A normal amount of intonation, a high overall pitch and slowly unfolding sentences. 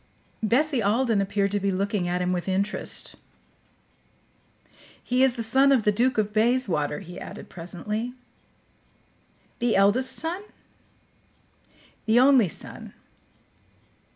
Yes: average, 4.3 semitones; high, 215 Hz; slow, 120 wpm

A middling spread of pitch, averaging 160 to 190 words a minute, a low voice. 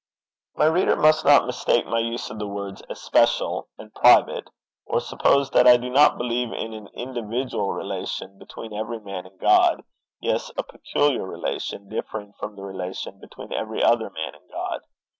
Yes: average, 3.7 semitones; average, 170 wpm; low, 110 Hz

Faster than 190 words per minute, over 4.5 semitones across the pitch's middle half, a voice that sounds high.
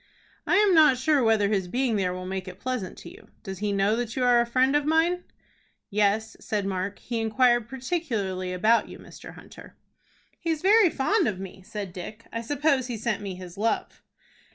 Yes: average, 200 wpm; average, 5.2 semitones; high, 225 Hz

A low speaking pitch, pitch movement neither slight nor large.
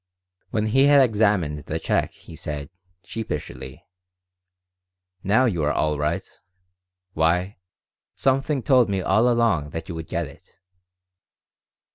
No: very low, 95 Hz; wide, 7.2 semitones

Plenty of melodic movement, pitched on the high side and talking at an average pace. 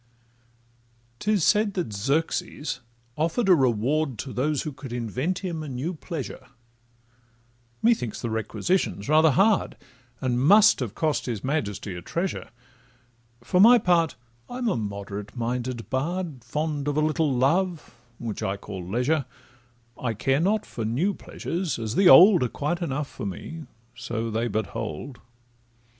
No: wide, 6.6 semitones; medium, 140 Hz; average, 150 wpm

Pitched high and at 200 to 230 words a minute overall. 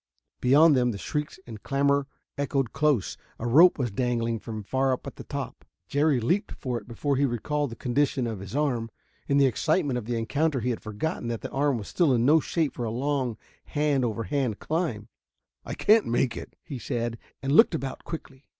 No: low, 130 Hz; fast, 205 wpm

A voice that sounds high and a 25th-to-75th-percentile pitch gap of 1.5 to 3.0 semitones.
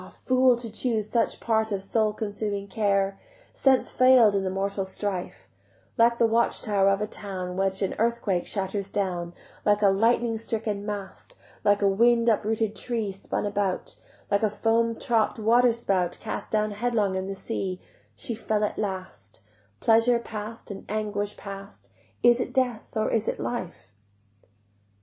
Yes: high, 210 Hz; average, 2.7 semitones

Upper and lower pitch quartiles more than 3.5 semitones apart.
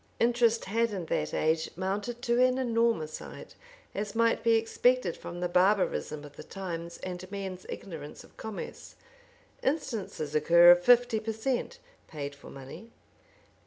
Yes: average, 5.3 semitones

